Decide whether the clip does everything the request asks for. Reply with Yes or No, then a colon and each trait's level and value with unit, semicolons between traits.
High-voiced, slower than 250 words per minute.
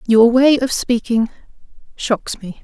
Yes: high, 235 Hz; slow, 135 wpm